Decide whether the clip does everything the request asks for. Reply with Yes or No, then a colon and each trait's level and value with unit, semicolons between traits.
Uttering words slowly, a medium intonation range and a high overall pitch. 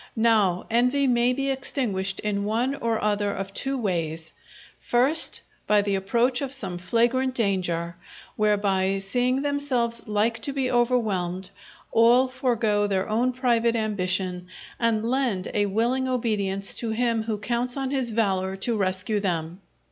No: average, 145 wpm; average, 4.2 semitones; high, 220 Hz